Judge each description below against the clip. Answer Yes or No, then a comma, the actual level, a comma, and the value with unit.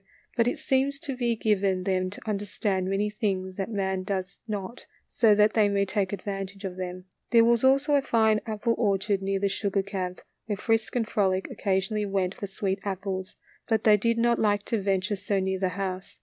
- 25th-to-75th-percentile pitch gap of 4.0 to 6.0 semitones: No, narrow, 2.4 semitones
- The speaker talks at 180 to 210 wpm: Yes, fast, 205 wpm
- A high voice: Yes, high, 200 Hz